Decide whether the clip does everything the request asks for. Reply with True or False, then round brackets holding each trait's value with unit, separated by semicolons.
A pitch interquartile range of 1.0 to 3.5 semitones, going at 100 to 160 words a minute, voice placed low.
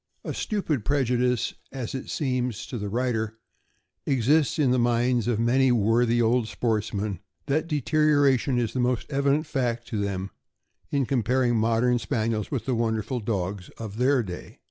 True (2.9 semitones; 155 wpm; 120 Hz)